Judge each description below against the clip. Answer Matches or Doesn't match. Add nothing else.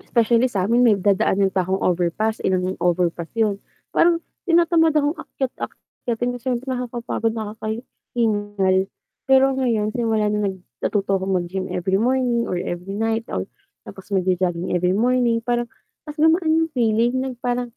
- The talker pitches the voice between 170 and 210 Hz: Doesn't match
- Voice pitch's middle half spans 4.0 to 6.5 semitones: Matches